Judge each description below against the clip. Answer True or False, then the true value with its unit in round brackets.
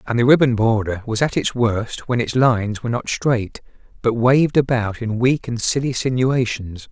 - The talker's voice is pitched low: True (120 Hz)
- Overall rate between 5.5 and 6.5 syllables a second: False (4.9 syllables/s)